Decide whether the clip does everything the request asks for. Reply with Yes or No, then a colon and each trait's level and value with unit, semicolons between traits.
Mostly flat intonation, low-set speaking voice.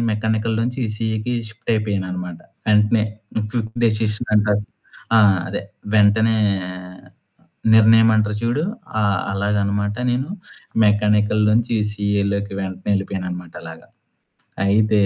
Yes: narrow, 1.5 semitones; low, 105 Hz